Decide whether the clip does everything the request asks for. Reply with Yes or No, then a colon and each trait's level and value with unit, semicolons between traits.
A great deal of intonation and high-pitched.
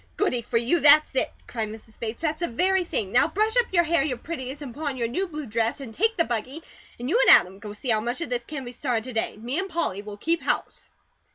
Yes: wide, 6.5 semitones; very high, 260 Hz